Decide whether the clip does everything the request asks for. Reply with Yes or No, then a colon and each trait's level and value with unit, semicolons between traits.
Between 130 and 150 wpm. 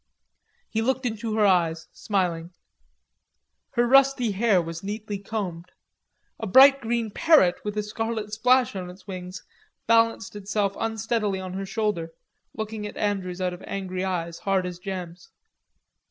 Yes: average, 145 wpm